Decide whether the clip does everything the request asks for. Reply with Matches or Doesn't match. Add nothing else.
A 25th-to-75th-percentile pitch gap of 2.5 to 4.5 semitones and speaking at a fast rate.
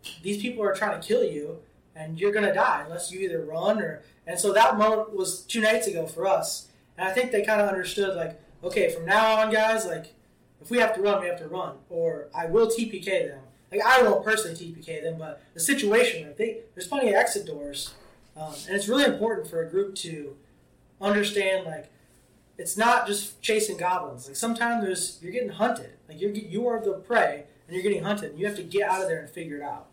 Doesn't match